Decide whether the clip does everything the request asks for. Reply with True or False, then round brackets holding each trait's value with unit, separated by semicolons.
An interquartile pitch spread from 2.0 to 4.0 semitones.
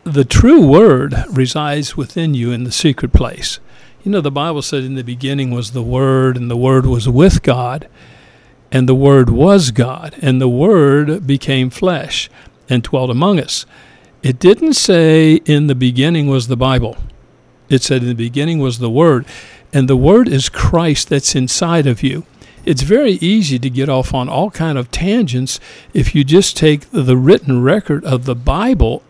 True (3.7 semitones)